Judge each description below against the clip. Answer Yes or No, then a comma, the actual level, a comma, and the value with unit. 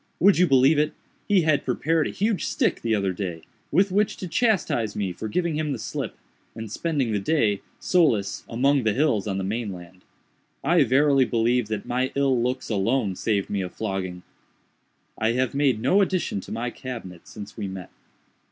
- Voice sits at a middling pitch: No, low, 120 Hz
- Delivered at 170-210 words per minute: Yes, average, 185 wpm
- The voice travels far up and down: Yes, wide, 6.8 semitones